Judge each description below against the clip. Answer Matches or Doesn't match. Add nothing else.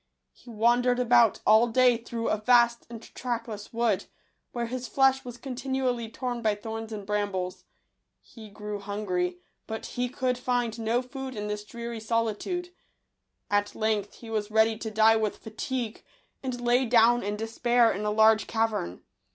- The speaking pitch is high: Matches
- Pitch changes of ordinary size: Doesn't match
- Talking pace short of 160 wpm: Doesn't match